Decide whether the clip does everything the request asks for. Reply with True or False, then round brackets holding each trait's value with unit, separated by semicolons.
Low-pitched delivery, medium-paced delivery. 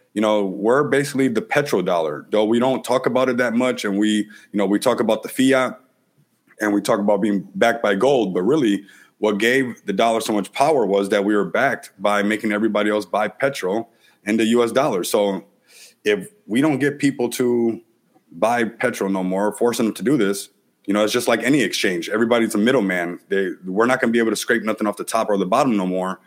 False (110 Hz; 230 wpm)